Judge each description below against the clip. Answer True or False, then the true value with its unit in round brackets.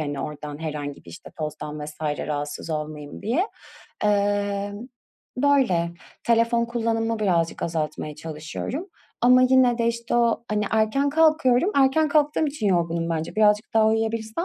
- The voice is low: False (215 Hz)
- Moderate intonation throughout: False (7.5 semitones)